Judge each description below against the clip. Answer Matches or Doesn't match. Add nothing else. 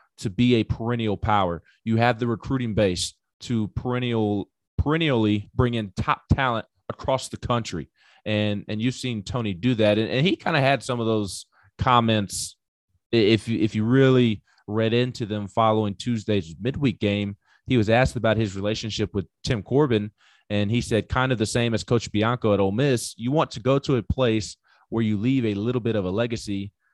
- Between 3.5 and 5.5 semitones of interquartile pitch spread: Doesn't match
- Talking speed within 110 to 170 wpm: Doesn't match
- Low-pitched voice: Matches